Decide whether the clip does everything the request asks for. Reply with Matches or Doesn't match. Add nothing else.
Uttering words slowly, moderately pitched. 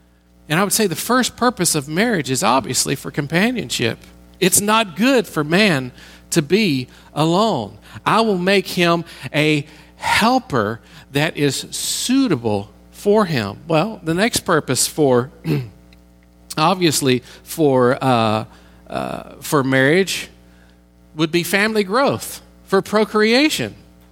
Matches